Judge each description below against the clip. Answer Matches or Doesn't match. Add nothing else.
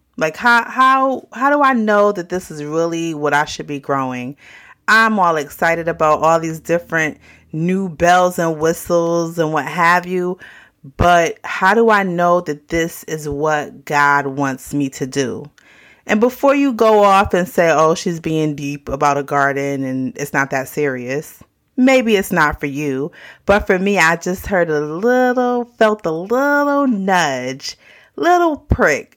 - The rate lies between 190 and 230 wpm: Doesn't match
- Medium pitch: Matches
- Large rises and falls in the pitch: Matches